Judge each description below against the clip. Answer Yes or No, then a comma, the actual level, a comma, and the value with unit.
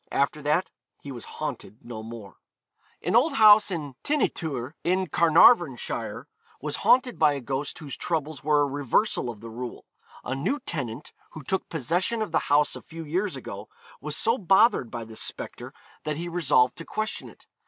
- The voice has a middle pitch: Yes, medium, 150 Hz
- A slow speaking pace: No, average, 185 wpm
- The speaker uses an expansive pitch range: Yes, wide, 6.0 semitones